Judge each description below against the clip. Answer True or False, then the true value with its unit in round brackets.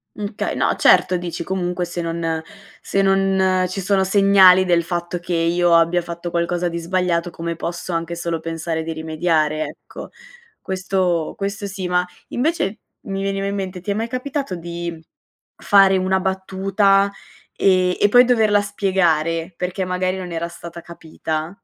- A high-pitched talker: False (180 Hz)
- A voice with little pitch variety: True (2.3 semitones)